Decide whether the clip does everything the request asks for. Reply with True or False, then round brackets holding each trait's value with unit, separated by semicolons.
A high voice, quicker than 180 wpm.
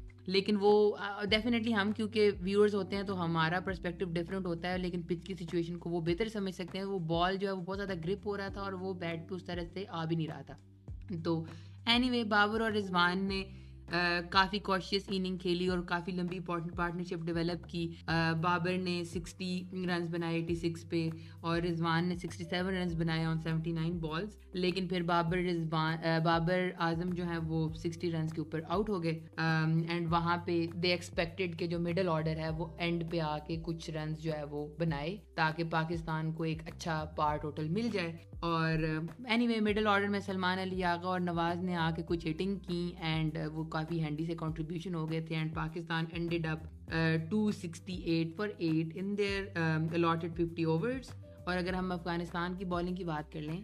False (175 Hz; 190 wpm)